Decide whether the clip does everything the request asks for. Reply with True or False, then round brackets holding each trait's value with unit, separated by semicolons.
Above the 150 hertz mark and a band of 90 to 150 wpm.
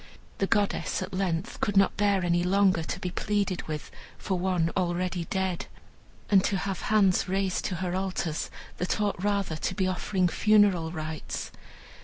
False (185 Hz; 165 wpm)